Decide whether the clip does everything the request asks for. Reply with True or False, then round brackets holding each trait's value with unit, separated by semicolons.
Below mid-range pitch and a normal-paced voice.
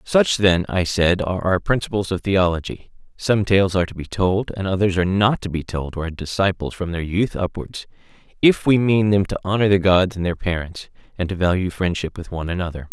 False (95 Hz; 215 wpm)